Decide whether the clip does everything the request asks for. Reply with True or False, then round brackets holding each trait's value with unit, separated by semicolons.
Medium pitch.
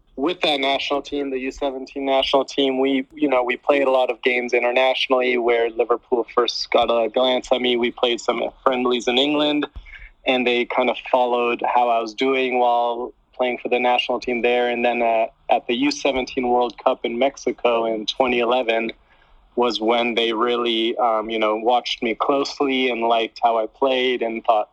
False (125 Hz)